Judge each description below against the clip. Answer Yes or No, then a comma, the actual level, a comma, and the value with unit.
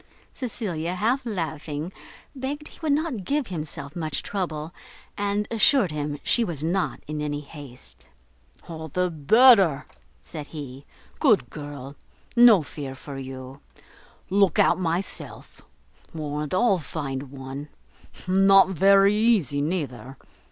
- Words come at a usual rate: No, slow, 125 wpm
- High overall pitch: No, medium, 165 Hz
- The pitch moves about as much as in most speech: No, wide, 5.7 semitones